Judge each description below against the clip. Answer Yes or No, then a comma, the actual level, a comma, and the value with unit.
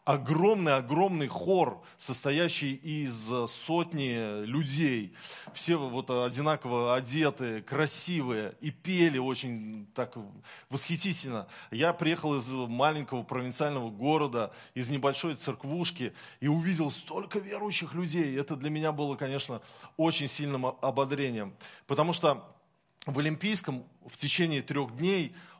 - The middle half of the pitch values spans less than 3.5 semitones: No, average, 4.2 semitones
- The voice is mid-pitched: Yes, medium, 145 Hz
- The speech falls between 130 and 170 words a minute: No, slow, 110 wpm